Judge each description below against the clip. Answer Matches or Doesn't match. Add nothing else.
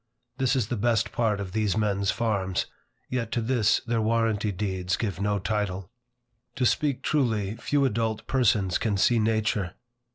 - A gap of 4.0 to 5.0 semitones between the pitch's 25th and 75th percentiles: Doesn't match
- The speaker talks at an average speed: Matches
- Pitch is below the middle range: Matches